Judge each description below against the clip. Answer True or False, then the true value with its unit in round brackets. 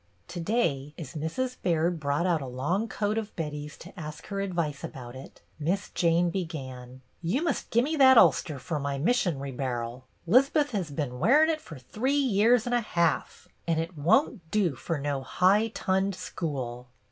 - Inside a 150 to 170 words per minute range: False (185 wpm)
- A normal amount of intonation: False (6.9 semitones)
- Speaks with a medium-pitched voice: True (170 Hz)